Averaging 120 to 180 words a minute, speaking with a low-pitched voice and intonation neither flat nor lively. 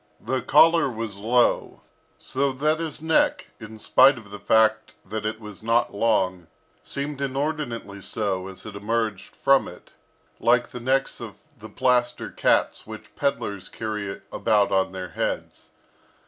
Yes: average, 145 wpm; low, 115 Hz; average, 4.5 semitones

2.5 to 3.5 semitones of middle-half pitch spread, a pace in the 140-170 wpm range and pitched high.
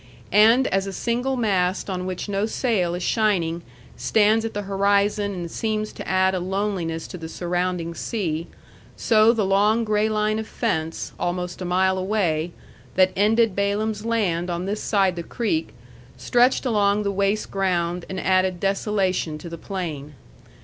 Yes: average, 3.2 semitones; average, 165 wpm; high, 195 Hz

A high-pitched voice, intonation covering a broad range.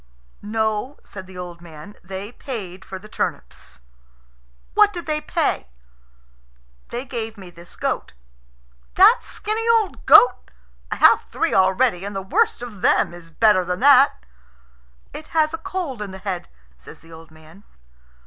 Yes: high, 210 Hz; wide, 8.0 semitones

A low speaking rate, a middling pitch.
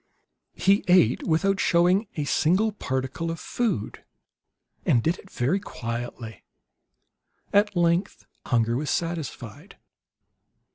Yes: slow, 105 wpm; medium, 165 Hz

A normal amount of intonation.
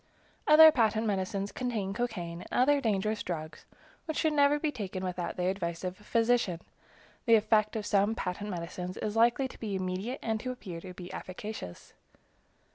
Yes: average, 4.5 semitones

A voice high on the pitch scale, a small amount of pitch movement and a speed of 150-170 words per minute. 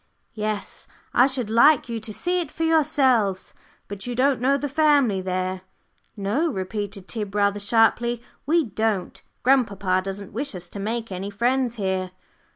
No: high, 225 Hz; average, 5.0 semitones; average, 160 wpm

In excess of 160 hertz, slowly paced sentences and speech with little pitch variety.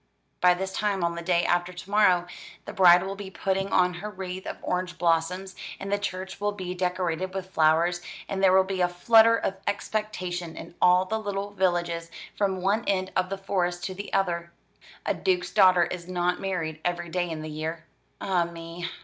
No: medium, 185 Hz; average, 200 wpm; narrow, 1.8 semitones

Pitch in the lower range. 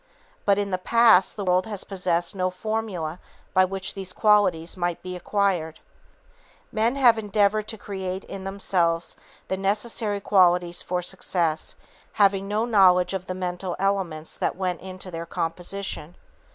No: high, 190 Hz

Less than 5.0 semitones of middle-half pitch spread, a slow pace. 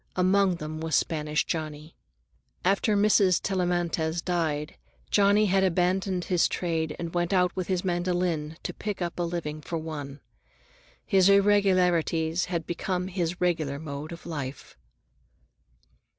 Yes: average, 2.7 semitones; slow, 130 wpm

